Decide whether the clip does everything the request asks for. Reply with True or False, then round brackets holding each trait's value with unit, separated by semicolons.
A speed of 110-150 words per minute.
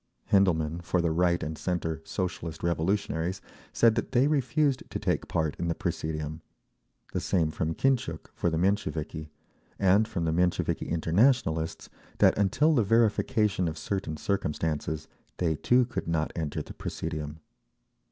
True (145 wpm)